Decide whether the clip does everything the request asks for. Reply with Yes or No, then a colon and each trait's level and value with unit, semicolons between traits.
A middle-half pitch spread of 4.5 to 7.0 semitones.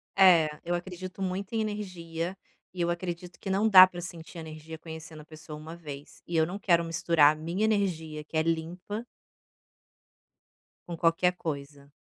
No: narrow, 2.6 semitones